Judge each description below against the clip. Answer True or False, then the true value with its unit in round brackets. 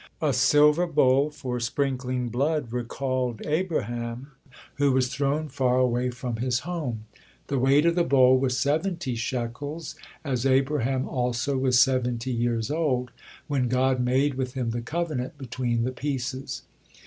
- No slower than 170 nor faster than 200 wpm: False (145 wpm)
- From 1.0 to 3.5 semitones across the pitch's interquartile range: True (2.5 semitones)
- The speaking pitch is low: True (130 Hz)